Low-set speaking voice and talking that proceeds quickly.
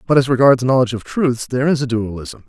Yes: low, 125 Hz; fast, 240 wpm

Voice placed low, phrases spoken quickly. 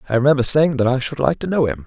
Yes: low, 125 Hz; fast, 320 wpm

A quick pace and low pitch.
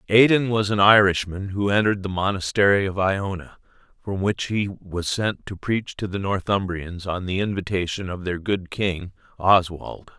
No: average, 165 wpm; very low, 95 Hz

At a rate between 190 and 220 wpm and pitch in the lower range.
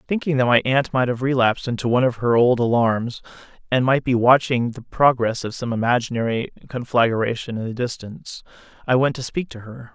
Yes: average, 195 wpm; low, 120 Hz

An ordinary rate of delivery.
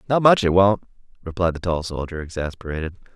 Yes: average, 170 wpm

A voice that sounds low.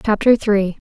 No: high, 210 Hz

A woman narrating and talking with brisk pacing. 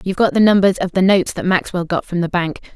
Yes: female; fast, 285 wpm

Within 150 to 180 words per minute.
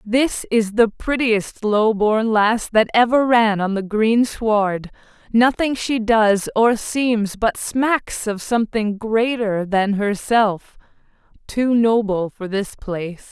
No: average, 140 wpm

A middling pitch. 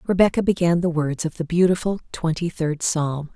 Yes: medium, 165 Hz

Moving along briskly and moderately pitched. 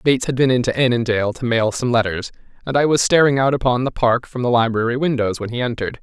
No: fast, 240 wpm; low, 125 Hz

